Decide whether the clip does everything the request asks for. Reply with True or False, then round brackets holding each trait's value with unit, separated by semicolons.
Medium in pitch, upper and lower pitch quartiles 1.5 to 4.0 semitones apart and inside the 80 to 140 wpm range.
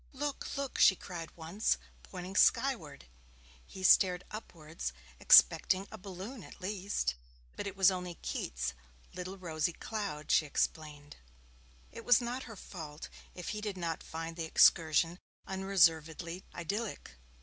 True (180 Hz; 3.7 semitones; 135 wpm)